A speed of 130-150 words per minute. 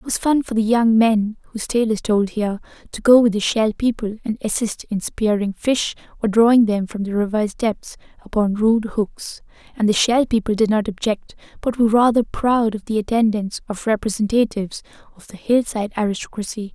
No: average, 190 wpm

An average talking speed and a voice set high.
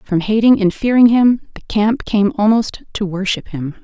Yes: average, 190 wpm; high, 210 Hz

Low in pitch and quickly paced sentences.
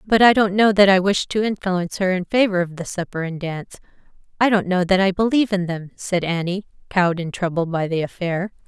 No: medium, 185 Hz; fast, 230 wpm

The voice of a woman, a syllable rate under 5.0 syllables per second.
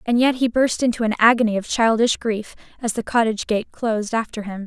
No: female; 5.9 syllables/s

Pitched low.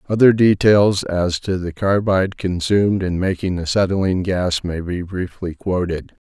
Yes: very low, 95 Hz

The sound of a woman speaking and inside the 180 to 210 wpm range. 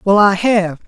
No: male; fast, 205 wpm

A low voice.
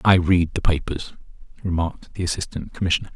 Yes: very low, 85 Hz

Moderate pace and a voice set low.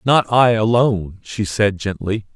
Yes: average, 155 wpm; low, 105 Hz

